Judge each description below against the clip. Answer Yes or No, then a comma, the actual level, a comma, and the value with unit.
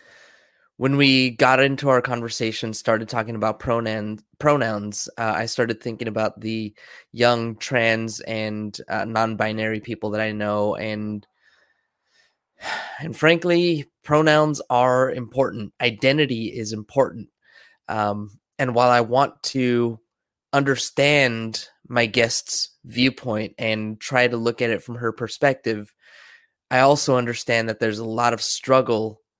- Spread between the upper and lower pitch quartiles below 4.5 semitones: Yes, average, 2.9 semitones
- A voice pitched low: Yes, low, 115 Hz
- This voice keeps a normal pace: No, slow, 130 wpm